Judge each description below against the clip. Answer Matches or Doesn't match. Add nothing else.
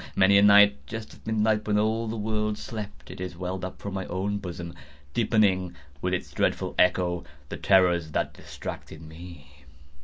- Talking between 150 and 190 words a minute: Matches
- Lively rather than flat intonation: Doesn't match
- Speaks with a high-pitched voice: Doesn't match